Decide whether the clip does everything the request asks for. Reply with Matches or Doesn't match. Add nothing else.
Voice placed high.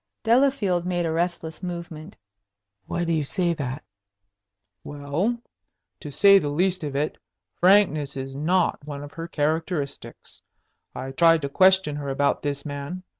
Doesn't match